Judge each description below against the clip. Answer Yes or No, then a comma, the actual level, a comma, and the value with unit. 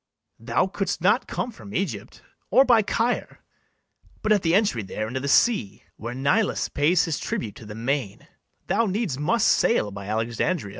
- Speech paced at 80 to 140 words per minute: No, average, 170 wpm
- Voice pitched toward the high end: No, medium, 155 Hz